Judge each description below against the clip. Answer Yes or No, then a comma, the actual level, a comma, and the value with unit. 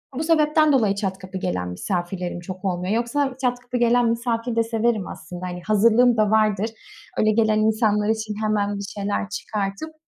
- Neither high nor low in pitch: No, high, 215 Hz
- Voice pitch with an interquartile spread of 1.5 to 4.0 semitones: Yes, average, 3.3 semitones